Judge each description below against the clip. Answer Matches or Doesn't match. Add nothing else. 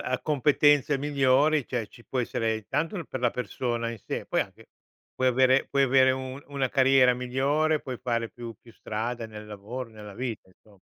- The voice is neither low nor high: Doesn't match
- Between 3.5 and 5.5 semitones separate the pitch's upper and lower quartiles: Doesn't match